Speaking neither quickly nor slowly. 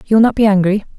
No: fast, 305 wpm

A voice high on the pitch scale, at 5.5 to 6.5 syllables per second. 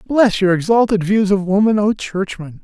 No: high, 200 Hz; 4.9 syllables/s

